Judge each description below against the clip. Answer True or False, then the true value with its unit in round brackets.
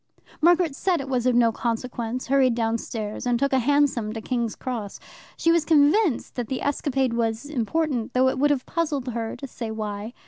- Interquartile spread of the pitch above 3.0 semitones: True (3.8 semitones)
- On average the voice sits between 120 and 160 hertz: False (255 Hz)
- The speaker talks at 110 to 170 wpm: False (200 wpm)